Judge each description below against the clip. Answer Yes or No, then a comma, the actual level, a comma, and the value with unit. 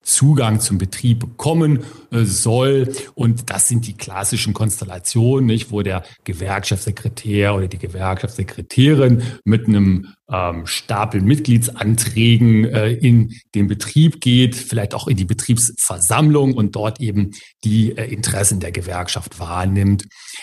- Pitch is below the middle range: Yes, low, 110 Hz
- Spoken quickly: No, slow, 125 wpm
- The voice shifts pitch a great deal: No, average, 3.3 semitones